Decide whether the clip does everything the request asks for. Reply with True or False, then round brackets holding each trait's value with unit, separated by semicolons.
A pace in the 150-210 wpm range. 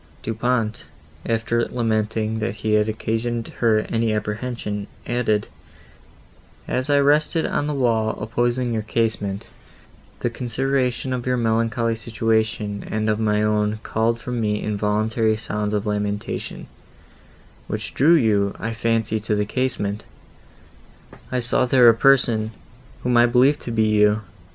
False (140 wpm)